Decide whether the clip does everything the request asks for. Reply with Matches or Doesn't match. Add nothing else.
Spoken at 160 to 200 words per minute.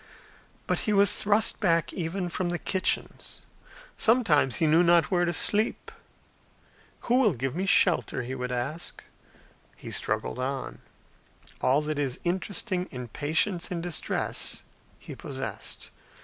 Doesn't match